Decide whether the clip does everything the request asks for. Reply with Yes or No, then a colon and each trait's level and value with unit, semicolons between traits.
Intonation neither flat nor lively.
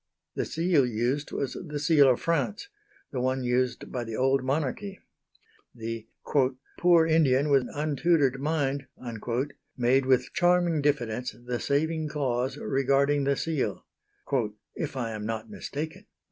Yes: average, 3.8 semitones